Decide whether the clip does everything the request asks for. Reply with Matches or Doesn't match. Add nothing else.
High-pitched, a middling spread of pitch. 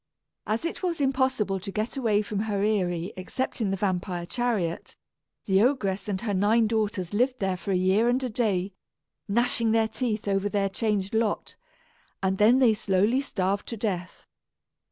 Matches